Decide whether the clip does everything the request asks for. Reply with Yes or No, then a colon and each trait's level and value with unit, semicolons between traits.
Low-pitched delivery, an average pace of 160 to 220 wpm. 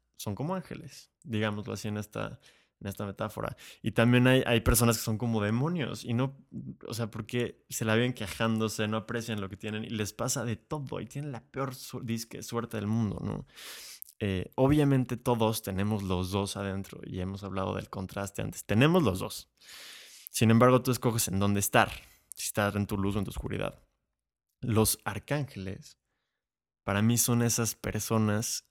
Yes: low, 110 Hz; average, 180 wpm